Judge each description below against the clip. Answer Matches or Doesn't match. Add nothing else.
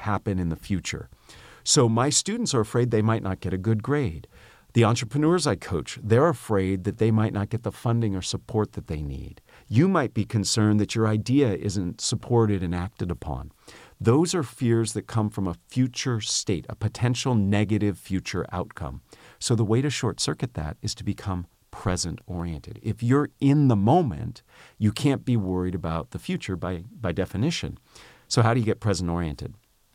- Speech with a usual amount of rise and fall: Matches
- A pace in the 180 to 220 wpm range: Matches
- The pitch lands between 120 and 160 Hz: Doesn't match